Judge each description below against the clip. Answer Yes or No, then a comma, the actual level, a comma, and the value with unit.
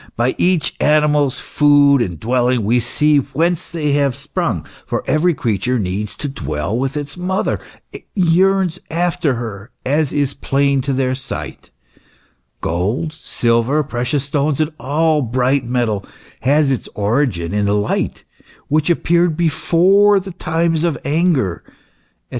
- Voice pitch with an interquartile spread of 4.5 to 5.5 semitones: Yes, average, 4.8 semitones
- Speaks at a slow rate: No, average, 145 wpm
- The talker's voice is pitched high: No, medium, 140 Hz